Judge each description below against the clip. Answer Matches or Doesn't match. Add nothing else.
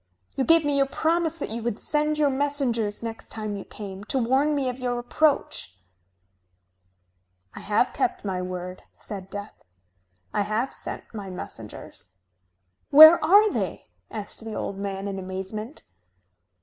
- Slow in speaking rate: Doesn't match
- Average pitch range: Doesn't match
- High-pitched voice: Matches